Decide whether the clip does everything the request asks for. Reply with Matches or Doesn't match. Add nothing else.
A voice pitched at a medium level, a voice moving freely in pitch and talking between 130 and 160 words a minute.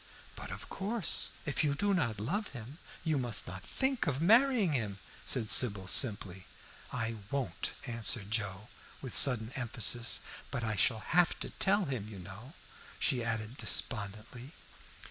Doesn't match